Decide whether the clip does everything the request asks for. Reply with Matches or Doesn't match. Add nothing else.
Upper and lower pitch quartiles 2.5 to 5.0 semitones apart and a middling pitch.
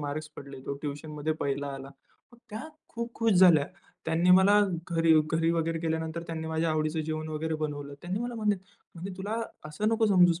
Matches